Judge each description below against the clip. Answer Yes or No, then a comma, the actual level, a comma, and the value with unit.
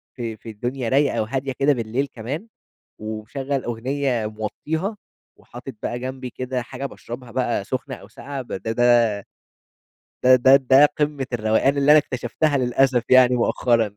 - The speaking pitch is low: Yes, low, 130 Hz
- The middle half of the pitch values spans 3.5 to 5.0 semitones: No, narrow, 2.6 semitones